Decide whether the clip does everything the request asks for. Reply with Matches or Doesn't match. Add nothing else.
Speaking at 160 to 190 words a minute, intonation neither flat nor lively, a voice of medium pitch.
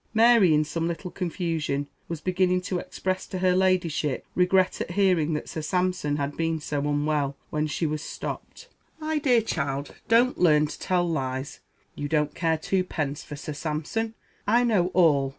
Matches